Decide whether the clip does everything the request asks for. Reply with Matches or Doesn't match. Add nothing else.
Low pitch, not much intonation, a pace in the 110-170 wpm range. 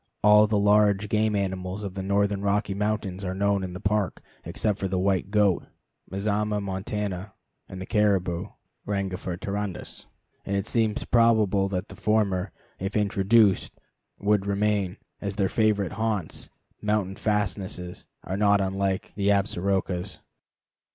Matches